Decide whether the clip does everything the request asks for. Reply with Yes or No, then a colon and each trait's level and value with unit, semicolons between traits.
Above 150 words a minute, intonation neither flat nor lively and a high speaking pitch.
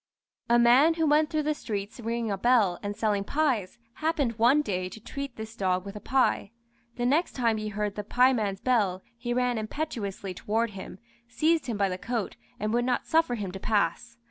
Yes: average, 200 wpm; average, 4.0 semitones; high, 230 Hz